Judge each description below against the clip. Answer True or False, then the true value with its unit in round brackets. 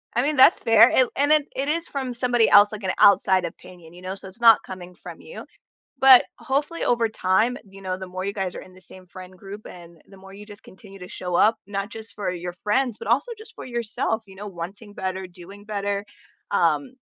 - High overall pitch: True (205 Hz)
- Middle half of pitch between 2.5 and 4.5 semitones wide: True (4.2 semitones)